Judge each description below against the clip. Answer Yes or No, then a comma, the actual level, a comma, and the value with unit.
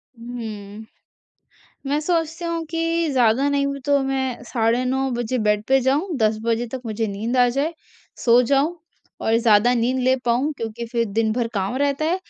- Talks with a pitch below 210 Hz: No, very high, 250 Hz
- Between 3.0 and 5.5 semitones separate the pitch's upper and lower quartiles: Yes, average, 3.6 semitones